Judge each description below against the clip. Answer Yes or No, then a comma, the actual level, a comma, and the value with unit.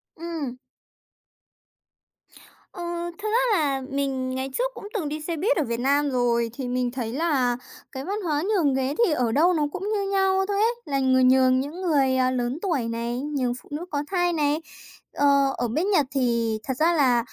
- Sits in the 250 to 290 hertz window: Yes, very high, 280 Hz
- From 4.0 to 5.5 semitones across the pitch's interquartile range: Yes, average, 5.1 semitones